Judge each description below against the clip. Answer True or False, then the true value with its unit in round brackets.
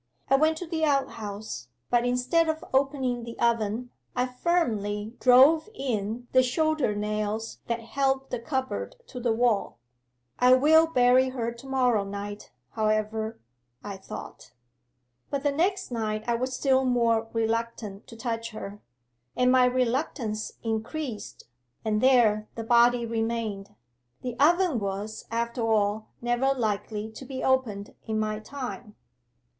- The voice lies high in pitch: True (235 Hz)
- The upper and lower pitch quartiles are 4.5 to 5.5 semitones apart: False (3.3 semitones)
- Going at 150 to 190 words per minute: False (140 wpm)